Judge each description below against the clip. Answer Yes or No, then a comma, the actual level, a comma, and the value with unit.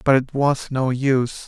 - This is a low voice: Yes, low, 130 Hz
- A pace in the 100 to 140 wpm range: No, fast, 205 wpm